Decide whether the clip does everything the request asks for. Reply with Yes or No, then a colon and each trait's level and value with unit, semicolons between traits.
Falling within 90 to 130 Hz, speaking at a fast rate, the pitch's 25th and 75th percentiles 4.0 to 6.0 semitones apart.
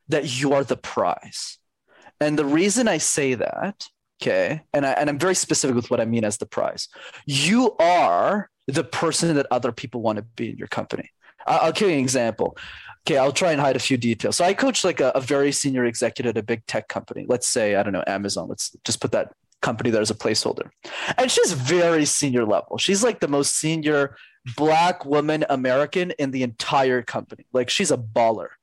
No: medium, 140 Hz; fast, 215 wpm; average, 4.5 semitones